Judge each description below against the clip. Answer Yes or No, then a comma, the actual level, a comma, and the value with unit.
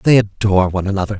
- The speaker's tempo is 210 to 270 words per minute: No, average, 200 wpm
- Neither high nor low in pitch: No, low, 100 Hz